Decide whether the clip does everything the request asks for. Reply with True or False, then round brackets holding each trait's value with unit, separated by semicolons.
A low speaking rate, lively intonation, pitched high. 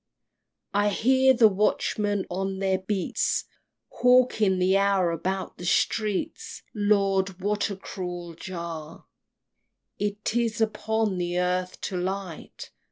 False (120 wpm; 2.5 semitones; 195 Hz)